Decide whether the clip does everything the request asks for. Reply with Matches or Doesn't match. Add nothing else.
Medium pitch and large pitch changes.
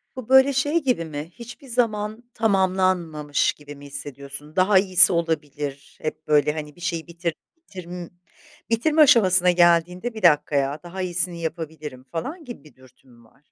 Matches